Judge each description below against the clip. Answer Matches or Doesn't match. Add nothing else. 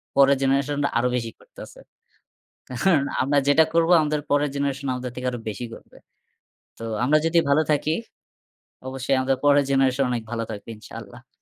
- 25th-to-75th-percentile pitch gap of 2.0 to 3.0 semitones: Matches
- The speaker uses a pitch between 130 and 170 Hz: Matches